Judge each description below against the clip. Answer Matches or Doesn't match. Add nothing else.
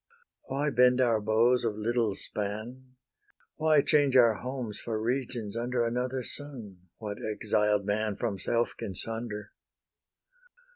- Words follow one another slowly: Matches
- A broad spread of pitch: Doesn't match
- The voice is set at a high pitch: Doesn't match